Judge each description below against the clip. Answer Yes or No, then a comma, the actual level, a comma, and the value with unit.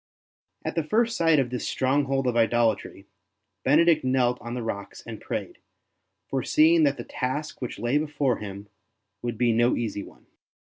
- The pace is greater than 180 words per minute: No, average, 165 wpm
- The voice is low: Yes, low, 130 Hz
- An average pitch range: Yes, average, 3.9 semitones